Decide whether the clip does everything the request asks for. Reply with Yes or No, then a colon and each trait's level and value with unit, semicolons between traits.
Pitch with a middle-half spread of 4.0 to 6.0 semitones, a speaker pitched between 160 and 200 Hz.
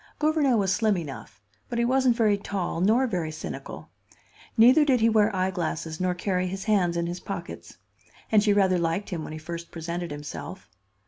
Yes: average, 4.5 semitones; high, 190 Hz